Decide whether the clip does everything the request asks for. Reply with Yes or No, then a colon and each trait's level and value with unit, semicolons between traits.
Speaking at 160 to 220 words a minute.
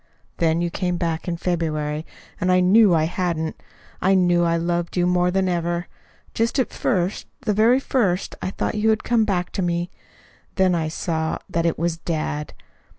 Yes: average, 185 wpm